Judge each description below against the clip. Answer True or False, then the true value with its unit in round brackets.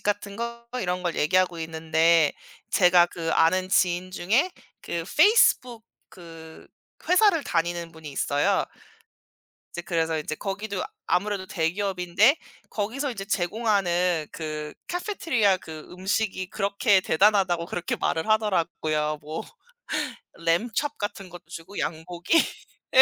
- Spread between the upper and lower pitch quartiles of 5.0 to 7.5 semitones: False (3.9 semitones)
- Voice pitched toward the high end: False (180 Hz)